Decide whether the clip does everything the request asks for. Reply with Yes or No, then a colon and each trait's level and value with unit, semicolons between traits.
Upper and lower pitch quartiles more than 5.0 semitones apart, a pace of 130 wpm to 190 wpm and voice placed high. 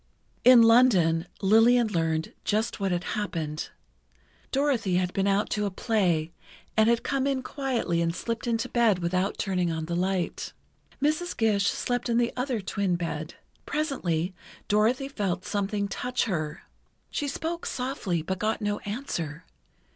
Yes: wide, 5.5 semitones; average, 150 wpm; high, 205 Hz